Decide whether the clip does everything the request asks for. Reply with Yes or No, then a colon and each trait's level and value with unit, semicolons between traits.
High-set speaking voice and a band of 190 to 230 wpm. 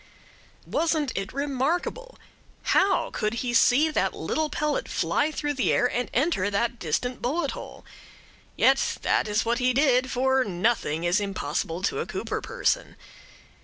No: very high, 250 Hz; average, 150 wpm